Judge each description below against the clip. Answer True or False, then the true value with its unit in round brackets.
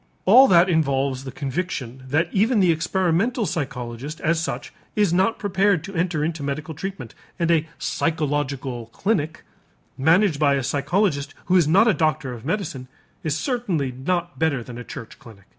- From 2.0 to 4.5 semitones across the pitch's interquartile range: False (5.1 semitones)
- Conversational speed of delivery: True (165 wpm)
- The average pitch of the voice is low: False (160 Hz)